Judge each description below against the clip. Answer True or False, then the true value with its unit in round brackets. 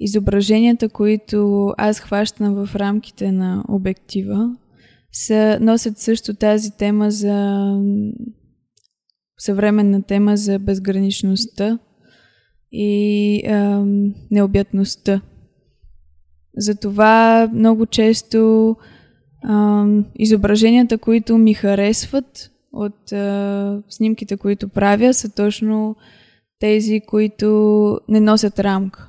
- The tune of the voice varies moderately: False (1.5 semitones)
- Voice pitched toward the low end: False (210 Hz)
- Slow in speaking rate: True (85 wpm)